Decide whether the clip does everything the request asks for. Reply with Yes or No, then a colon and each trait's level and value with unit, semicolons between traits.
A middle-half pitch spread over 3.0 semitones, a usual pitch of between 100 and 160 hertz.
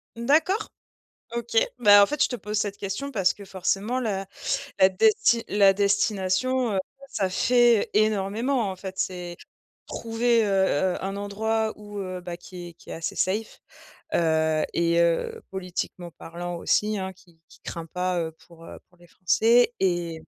No: average, 4.0 semitones; high, 200 Hz